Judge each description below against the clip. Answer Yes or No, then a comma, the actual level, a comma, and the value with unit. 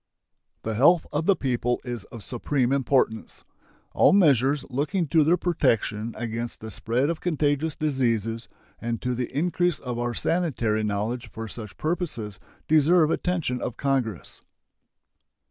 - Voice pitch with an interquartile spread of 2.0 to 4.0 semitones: No, average, 5.2 semitones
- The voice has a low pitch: Yes, low, 125 Hz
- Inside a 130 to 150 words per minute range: Yes, average, 140 wpm